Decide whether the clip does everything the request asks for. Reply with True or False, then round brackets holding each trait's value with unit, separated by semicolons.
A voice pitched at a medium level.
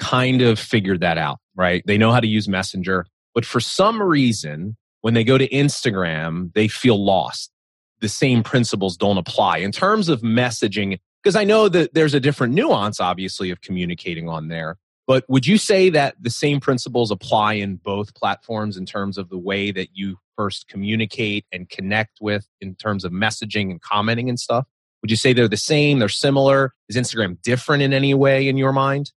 False (110 Hz)